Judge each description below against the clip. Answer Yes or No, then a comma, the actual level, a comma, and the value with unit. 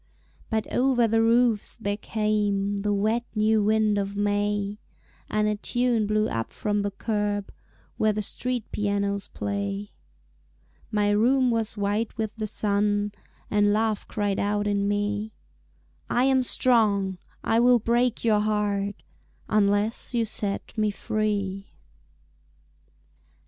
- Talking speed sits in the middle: No, slow, 130 wpm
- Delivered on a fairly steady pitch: Yes, narrow, 1.5 semitones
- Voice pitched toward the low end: No, high, 210 Hz